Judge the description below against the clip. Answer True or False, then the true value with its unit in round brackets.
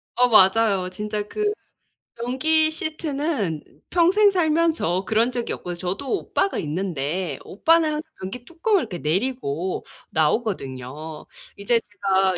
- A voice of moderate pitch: False (215 Hz)